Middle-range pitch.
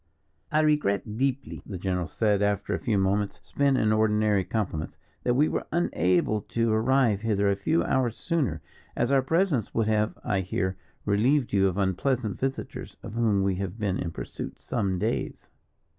No: low, 105 Hz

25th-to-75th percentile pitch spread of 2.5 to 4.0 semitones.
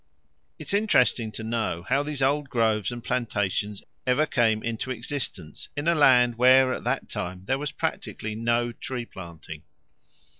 Yes: average, 3.6 semitones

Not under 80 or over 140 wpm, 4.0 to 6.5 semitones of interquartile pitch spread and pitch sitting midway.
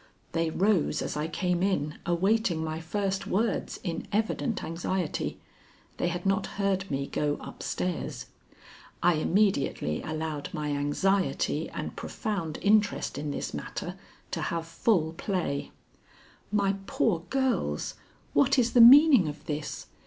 Yes: slow, 135 wpm; average, 4.5 semitones; medium, 175 Hz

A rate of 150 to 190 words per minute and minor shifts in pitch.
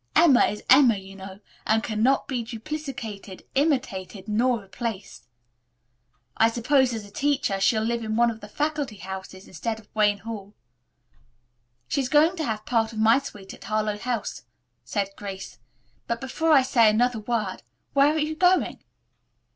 No: average, 165 wpm; average, 4.2 semitones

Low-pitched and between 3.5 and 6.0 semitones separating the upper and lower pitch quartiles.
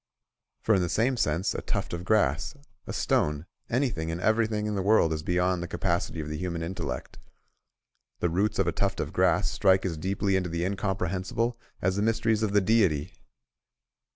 Yes: very low, 95 Hz; average, 4.0 semitones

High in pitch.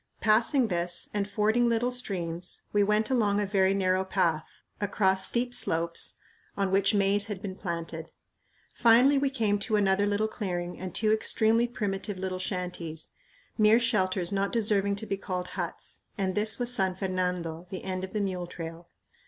Yes: high, 195 Hz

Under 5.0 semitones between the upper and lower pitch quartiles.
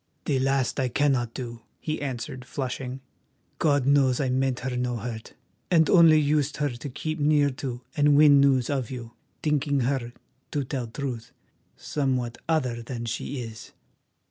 Yes: average, 2.8 semitones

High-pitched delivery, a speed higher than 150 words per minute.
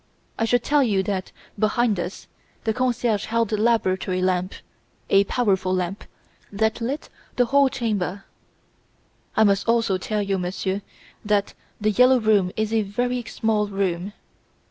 No: high, 210 Hz; average, 145 wpm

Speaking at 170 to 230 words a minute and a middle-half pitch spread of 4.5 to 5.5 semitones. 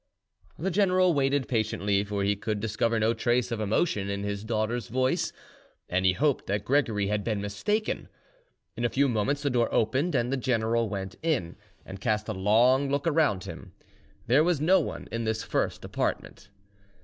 Yes: average, 180 wpm; average, 5.1 semitones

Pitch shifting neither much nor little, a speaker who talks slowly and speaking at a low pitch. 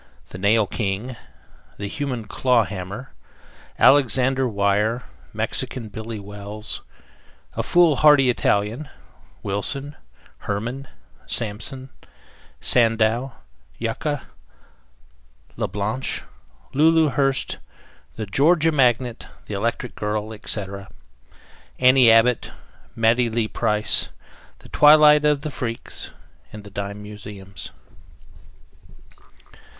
Yes: average, 4.4 semitones; slow, 90 wpm; low, 115 Hz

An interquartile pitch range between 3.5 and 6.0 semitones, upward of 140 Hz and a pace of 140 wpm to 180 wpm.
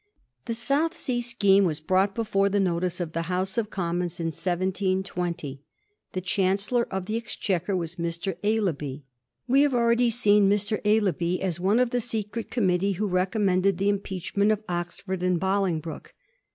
No: average, 3.1 semitones; high, 190 Hz; average, 165 wpm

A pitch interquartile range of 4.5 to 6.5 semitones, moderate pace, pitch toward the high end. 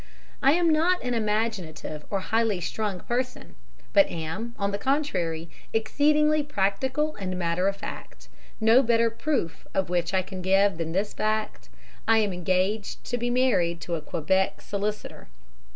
Yes: average, 4.9 semitones; average, 155 wpm; high, 205 Hz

